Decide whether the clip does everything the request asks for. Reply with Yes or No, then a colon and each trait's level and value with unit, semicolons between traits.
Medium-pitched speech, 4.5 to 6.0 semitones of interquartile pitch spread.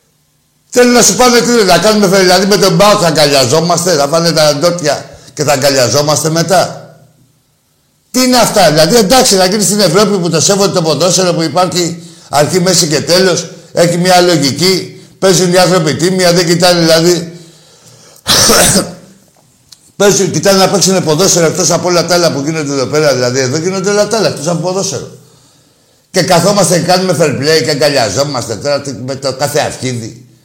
No: medium, 170 Hz; average, 4.0 semitones